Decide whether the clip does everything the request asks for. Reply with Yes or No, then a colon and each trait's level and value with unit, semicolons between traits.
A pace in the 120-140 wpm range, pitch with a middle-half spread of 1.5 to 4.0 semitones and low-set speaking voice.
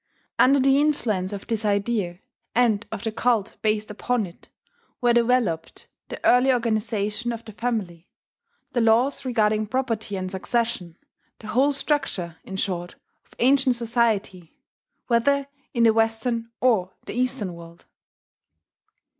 No: slow, 135 wpm; average, 3.5 semitones; high, 225 Hz